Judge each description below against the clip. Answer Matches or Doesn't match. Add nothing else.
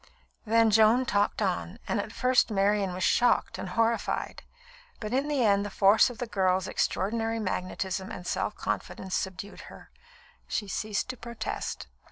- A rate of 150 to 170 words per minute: Matches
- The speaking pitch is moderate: Doesn't match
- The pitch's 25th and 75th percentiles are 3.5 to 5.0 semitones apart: Doesn't match